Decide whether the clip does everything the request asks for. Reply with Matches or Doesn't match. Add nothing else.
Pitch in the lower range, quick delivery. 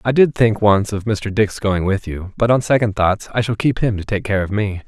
Matches